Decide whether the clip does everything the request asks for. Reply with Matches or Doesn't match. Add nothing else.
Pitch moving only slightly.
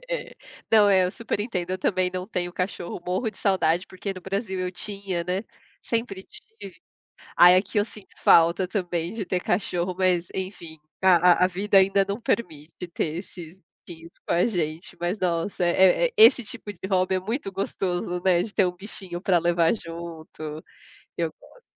Matches